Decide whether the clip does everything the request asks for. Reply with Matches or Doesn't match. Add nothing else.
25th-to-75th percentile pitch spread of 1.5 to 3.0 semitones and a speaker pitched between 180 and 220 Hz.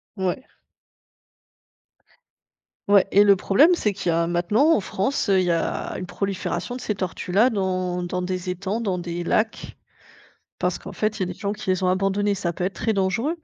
Matches